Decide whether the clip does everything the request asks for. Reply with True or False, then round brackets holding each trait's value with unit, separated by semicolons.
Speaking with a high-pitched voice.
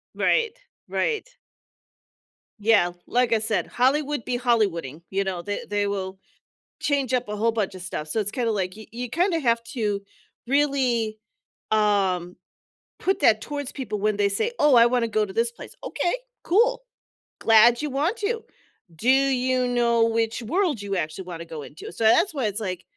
True (230 Hz)